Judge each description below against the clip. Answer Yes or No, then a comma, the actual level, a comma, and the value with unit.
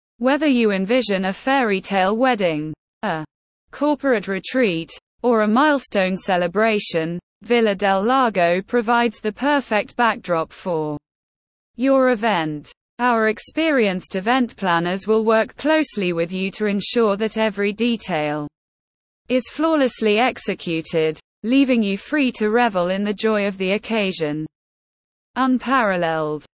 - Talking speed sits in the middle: No, slow, 120 wpm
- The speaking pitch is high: Yes, high, 215 Hz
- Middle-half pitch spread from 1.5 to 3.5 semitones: No, average, 4.9 semitones